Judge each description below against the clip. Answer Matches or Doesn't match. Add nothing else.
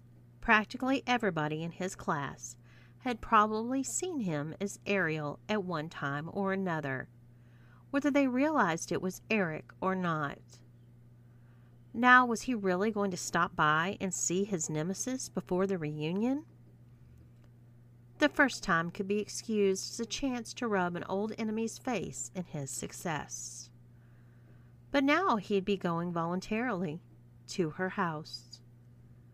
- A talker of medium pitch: Matches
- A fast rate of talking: Doesn't match